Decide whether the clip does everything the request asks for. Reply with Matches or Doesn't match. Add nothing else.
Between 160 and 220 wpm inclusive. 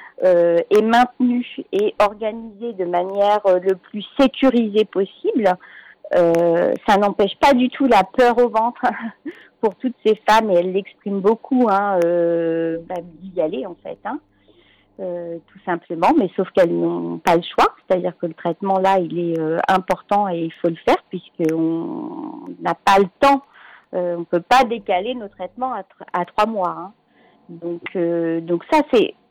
Matches